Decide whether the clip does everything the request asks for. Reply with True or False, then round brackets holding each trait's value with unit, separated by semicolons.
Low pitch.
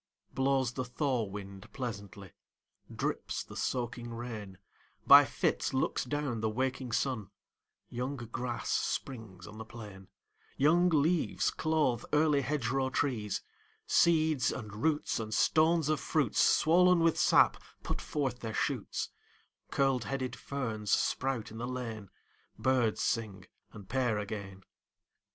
True (125 Hz)